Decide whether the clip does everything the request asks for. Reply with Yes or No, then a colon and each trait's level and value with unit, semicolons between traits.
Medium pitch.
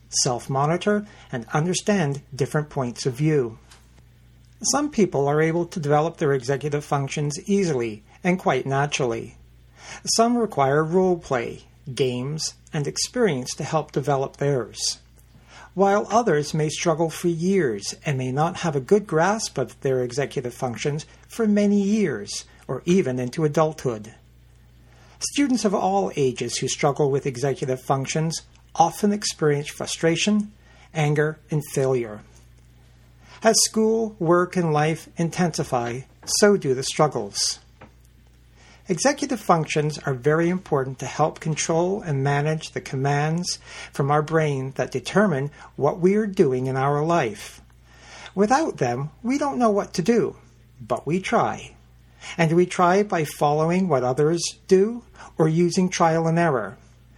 Yes: medium, 150 Hz